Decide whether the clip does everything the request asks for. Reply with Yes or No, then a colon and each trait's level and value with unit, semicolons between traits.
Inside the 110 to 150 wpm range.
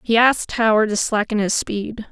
No: average, 200 wpm